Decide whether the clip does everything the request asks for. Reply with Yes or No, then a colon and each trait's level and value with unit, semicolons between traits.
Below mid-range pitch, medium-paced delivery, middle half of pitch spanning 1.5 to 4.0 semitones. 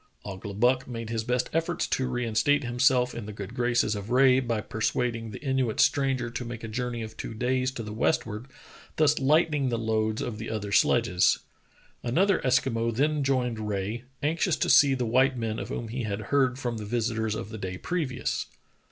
Yes: low, 120 Hz; average, 190 wpm; average, 3.0 semitones